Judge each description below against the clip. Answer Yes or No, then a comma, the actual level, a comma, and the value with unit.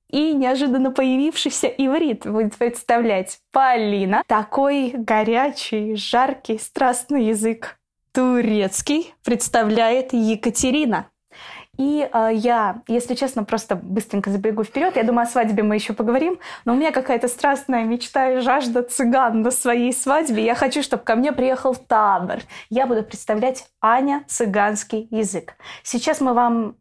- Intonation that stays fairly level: No, average, 3.2 semitones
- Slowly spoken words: No, average, 130 wpm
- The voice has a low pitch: No, high, 245 Hz